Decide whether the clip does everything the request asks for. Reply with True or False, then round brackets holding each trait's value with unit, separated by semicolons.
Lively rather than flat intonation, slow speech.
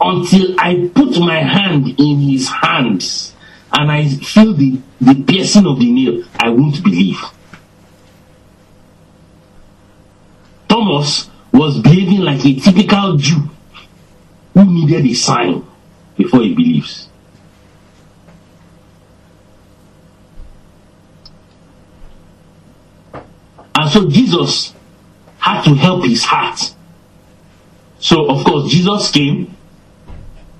True (6.3 semitones; 90 wpm)